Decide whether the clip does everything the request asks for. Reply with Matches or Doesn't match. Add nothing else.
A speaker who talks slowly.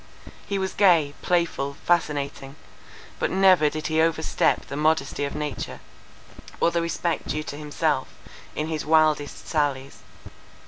Matches